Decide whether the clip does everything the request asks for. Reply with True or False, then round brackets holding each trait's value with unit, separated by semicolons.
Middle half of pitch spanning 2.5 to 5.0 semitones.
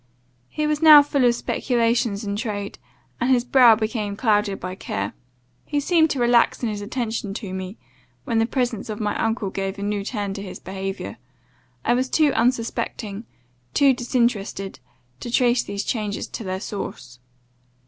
True (3.6 semitones)